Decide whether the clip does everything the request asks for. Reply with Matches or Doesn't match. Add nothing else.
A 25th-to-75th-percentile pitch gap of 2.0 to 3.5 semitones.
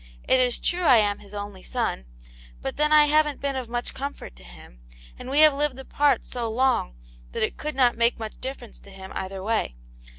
Doesn't match